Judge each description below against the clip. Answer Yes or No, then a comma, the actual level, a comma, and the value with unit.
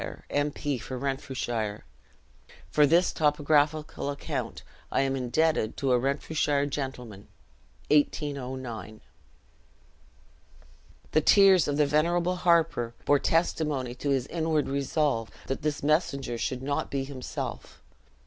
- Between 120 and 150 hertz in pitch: Yes, medium, 140 Hz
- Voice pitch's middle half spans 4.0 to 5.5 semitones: No, average, 2.9 semitones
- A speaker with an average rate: No, slow, 115 wpm